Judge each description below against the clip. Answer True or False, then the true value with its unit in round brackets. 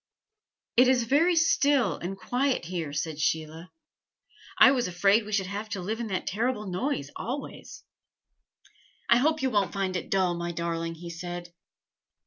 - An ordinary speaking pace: True (160 wpm)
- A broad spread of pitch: True (6.1 semitones)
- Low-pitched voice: False (195 Hz)